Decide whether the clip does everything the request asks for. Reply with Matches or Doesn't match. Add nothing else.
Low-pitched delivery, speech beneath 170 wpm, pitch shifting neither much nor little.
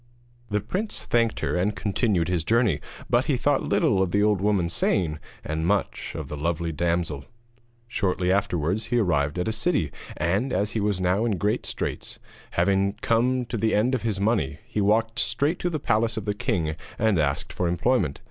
Doesn't match